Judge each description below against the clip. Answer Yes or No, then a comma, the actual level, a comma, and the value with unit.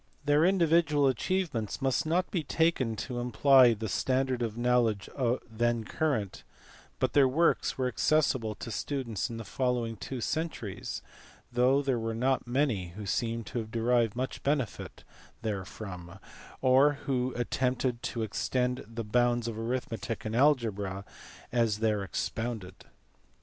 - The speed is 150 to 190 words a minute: No, average, 140 wpm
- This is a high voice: No, low, 120 Hz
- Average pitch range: Yes, average, 3.2 semitones